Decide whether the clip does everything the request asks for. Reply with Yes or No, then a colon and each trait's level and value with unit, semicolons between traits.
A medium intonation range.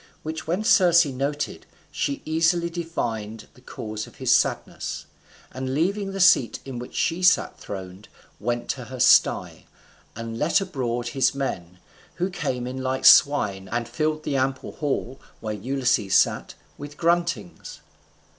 No: wide, 5.8 semitones